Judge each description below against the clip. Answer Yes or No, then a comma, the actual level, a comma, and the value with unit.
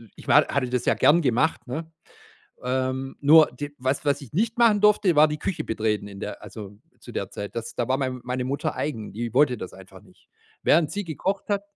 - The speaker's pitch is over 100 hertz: Yes, low, 135 Hz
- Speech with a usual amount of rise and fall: Yes, average, 4.6 semitones